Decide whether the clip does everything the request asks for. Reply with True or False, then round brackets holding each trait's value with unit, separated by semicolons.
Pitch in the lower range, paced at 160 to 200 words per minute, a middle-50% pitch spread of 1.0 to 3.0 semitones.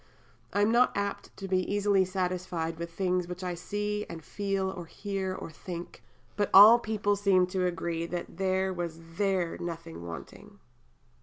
False (185 Hz; 170 wpm; 2.7 semitones)